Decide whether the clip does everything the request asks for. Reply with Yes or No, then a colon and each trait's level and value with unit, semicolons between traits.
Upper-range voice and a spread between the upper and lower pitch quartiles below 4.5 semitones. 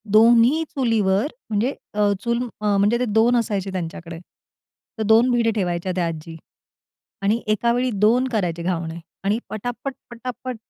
Yes: high, 215 Hz; average, 3.9 semitones